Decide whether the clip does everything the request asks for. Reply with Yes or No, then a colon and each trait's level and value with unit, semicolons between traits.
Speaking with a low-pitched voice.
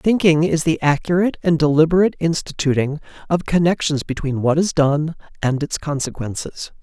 No: medium, 155 Hz